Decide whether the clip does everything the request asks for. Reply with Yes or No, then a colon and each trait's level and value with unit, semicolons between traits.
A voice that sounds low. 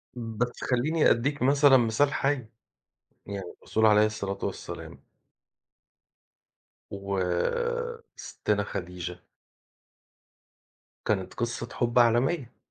Yes: low, 120 Hz